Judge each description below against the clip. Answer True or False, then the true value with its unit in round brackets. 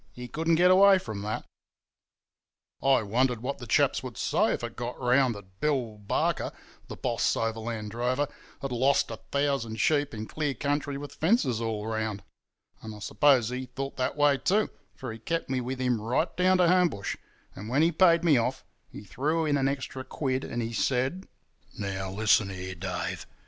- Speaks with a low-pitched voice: True (130 Hz)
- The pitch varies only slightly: False (4.7 semitones)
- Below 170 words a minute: False (185 wpm)